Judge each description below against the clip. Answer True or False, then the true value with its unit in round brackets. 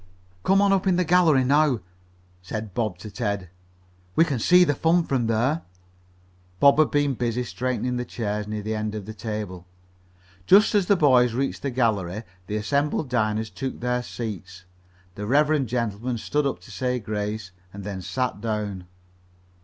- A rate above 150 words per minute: True (170 wpm)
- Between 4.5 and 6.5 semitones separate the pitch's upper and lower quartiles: True (5.0 semitones)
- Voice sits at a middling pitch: False (120 Hz)